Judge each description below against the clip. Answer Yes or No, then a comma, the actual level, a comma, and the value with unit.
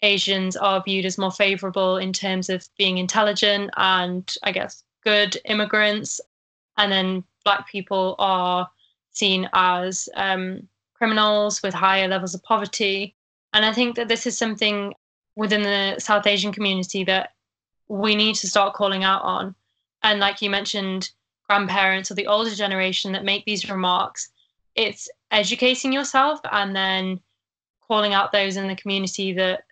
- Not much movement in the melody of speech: Yes, narrow, 1.8 semitones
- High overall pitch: Yes, high, 200 Hz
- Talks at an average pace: Yes, average, 150 wpm